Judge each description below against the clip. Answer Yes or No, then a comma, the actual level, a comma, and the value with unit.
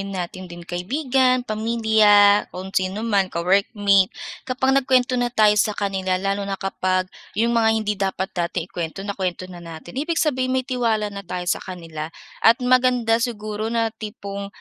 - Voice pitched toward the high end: Yes, high, 205 Hz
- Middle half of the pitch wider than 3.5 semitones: Yes, average, 4.0 semitones